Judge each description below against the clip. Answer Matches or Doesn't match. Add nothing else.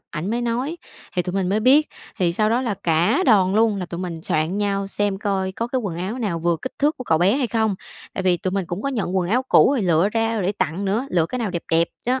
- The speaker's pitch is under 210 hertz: Matches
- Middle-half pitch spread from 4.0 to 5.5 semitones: Matches